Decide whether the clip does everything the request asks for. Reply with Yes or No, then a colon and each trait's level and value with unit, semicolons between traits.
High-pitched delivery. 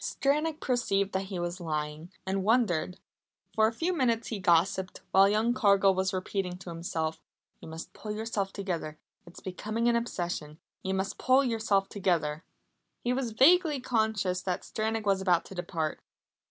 Yes: high, 195 Hz